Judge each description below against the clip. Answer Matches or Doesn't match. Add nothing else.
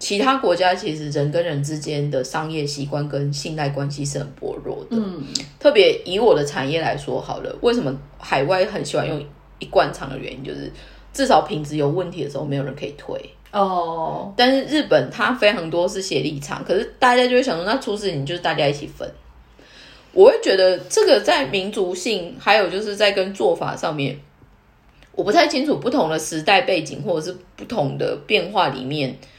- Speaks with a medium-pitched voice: Matches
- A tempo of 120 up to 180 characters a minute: Doesn't match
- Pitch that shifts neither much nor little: Doesn't match